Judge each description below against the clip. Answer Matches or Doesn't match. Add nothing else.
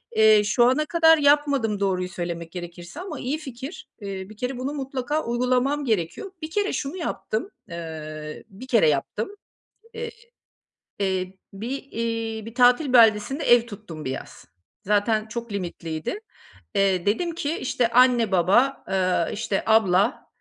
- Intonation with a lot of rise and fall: Matches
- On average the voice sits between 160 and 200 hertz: Doesn't match